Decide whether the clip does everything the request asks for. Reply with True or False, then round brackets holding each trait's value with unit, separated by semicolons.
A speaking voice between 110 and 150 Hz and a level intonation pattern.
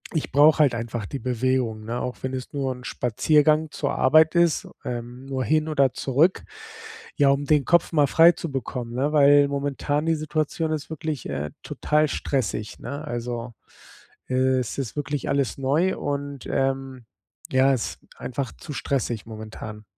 False (135 Hz; 3.1 semitones)